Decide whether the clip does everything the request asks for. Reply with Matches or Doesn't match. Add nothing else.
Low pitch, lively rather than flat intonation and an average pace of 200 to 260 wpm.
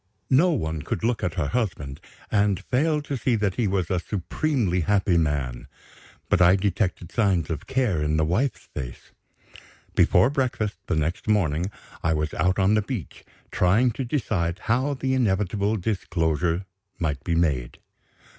Doesn't match